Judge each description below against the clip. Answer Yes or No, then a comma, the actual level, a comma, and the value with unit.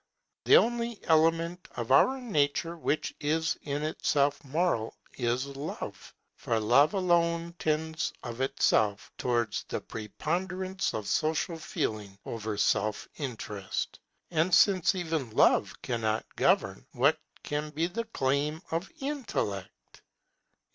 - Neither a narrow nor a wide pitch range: No, wide, 6.4 semitones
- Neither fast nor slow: No, slow, 120 wpm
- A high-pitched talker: No, medium, 155 Hz